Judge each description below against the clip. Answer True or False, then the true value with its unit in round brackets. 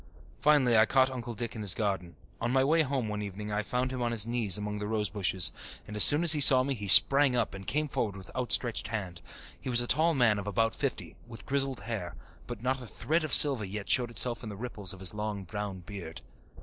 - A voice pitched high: False (115 Hz)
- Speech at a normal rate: False (240 wpm)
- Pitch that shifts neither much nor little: True (4.0 semitones)